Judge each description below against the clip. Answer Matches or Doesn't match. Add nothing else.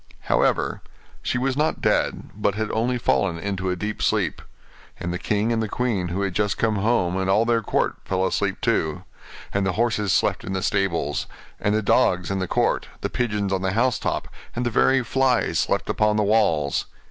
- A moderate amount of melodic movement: Matches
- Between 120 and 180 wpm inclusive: Doesn't match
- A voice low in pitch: Matches